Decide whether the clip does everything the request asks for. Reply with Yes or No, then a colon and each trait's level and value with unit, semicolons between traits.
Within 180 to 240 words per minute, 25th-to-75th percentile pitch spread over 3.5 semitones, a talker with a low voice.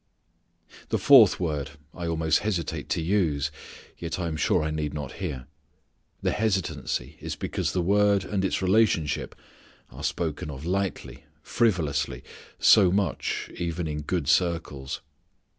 No: average, 140 wpm; average, 4.2 semitones; very low, 85 Hz